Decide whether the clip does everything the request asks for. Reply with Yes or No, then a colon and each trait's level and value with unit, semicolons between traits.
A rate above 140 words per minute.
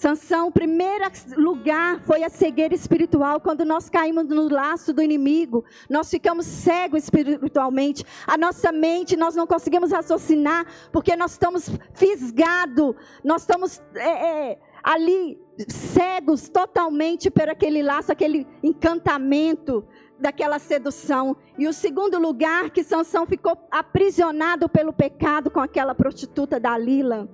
No: average, 130 wpm